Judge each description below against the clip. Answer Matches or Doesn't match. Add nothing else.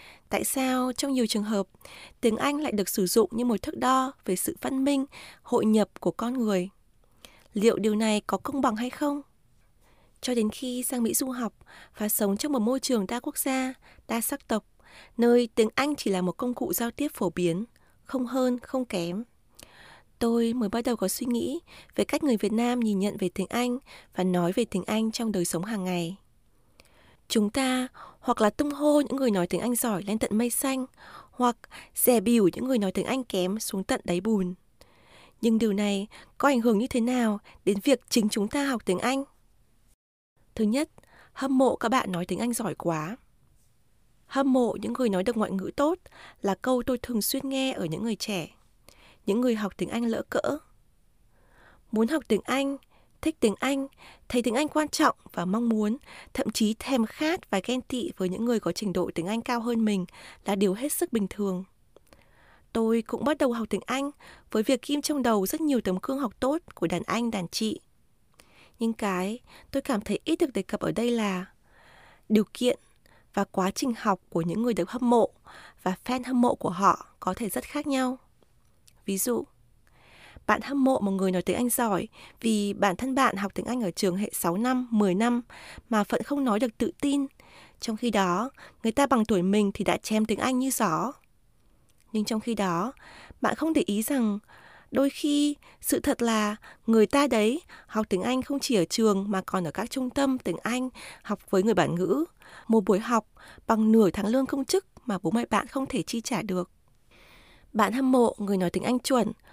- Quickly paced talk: Doesn't match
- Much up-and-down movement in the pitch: Doesn't match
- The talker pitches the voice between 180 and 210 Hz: Doesn't match